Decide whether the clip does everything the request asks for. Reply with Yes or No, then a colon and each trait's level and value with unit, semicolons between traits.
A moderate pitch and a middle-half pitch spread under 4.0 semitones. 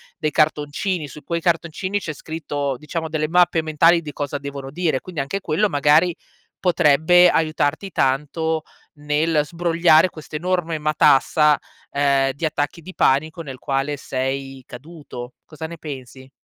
Yes: medium, 155 Hz; average, 2.8 semitones